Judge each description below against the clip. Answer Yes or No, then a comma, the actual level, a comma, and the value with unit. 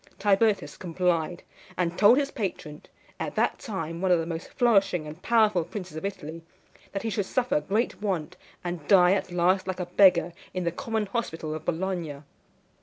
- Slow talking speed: No, average, 180 wpm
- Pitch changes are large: No, average, 3.4 semitones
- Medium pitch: Yes, medium, 180 Hz